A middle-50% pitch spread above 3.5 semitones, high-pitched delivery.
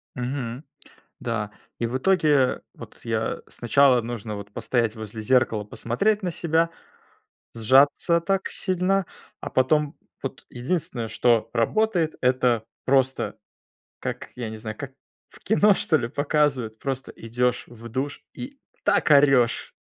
No: average, 4.8 semitones; low, 130 Hz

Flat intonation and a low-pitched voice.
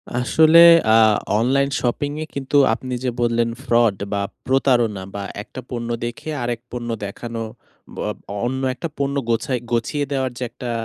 Yes: narrow, 2.3 semitones; low, 120 Hz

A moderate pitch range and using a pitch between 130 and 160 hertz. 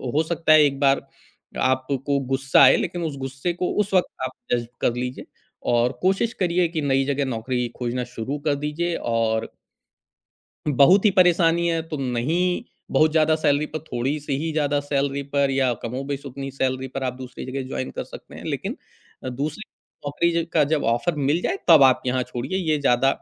Yes: average, 3.4 semitones; medium, 140 Hz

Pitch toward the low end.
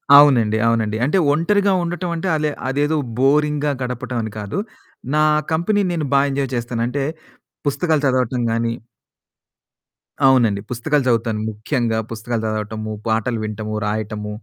Yes: low, 125 Hz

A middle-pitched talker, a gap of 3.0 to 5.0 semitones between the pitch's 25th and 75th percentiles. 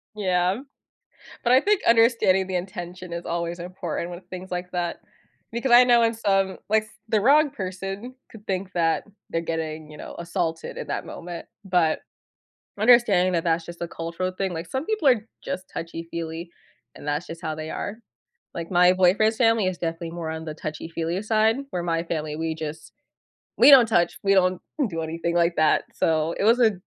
Yes: medium, 180 Hz; average, 4.0 semitones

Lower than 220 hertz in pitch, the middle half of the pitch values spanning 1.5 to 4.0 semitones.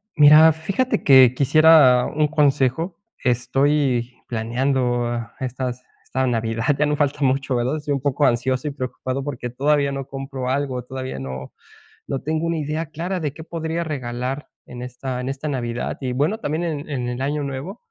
Yes: low, 135 Hz; average, 3.1 semitones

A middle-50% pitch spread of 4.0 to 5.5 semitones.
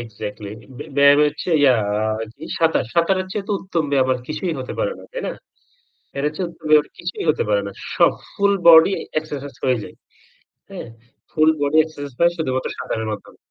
Yes: average, 4.5 semitones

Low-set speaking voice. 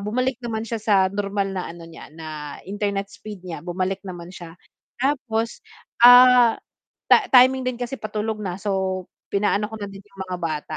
No: high, 205 Hz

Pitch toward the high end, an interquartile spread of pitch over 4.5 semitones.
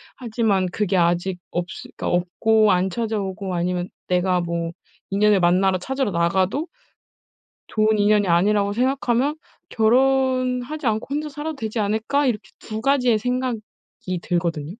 Yes: high, 210 Hz; wide, 5.5 semitones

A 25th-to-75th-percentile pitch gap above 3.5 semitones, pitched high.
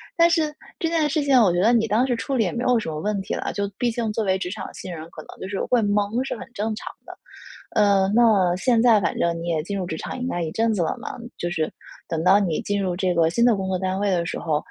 Yes: average, 4.7 semitones; high, 200 Hz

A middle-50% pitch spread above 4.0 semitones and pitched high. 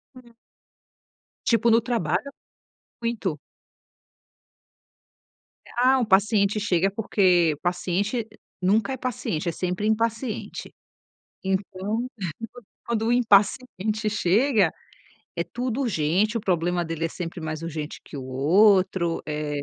Yes: average, 4.9 semitones; high, 200 Hz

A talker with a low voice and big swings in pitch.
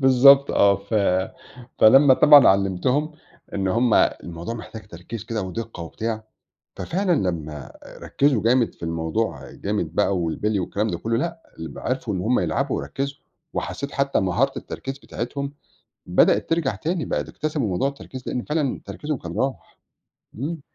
Yes: low, 115 Hz; wide, 6.4 semitones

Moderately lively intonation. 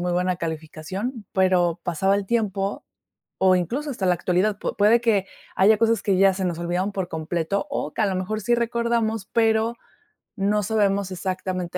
Yes: average, 3.2 semitones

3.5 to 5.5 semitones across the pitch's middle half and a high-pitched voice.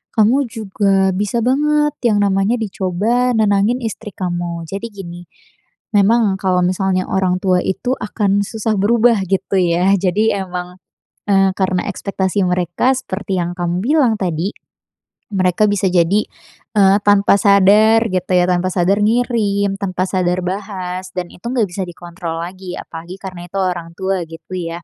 No: average, 2.7 semitones; high, 195 Hz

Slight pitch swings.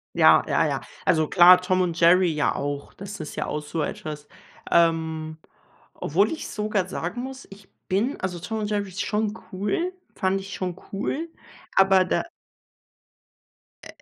No: average, 3.7 semitones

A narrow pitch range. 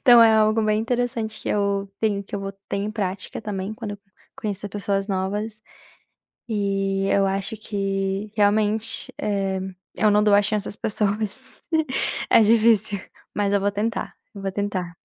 Yes: narrow, 1.5 semitones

